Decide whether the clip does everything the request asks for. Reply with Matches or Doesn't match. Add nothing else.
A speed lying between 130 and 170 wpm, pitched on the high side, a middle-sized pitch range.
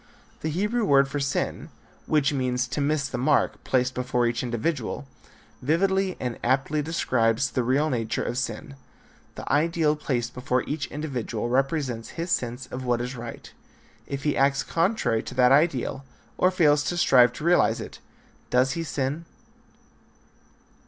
Doesn't match